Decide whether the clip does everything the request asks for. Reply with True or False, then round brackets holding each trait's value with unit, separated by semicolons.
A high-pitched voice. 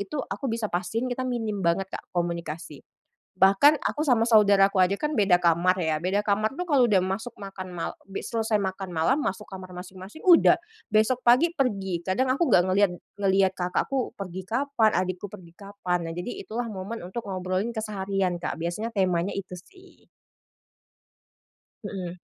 True (195 Hz)